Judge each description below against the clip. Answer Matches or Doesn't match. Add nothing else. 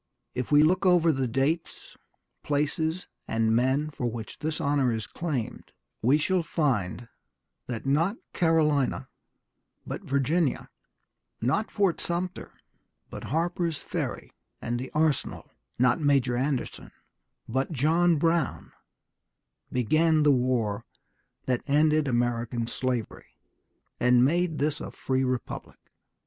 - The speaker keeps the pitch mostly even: Doesn't match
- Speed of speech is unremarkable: Doesn't match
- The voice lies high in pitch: Doesn't match